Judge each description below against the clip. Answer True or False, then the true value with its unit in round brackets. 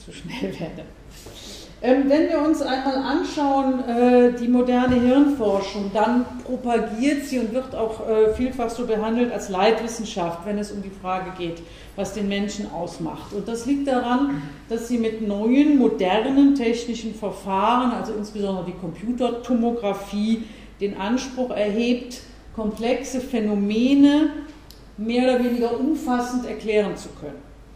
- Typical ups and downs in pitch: True (3.4 semitones)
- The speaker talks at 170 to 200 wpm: False (130 wpm)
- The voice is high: True (235 Hz)